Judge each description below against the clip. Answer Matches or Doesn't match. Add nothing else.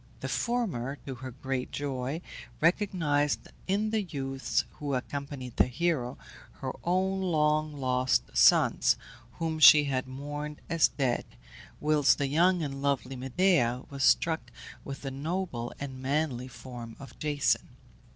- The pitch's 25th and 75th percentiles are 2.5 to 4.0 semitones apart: Matches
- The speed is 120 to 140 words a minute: Matches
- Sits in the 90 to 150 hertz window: Matches